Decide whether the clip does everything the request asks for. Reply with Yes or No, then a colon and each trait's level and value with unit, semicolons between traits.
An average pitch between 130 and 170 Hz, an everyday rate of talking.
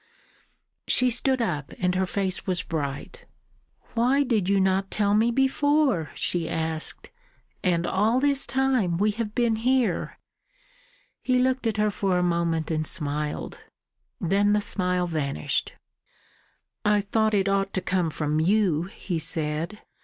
No: high, 195 Hz; average, 145 wpm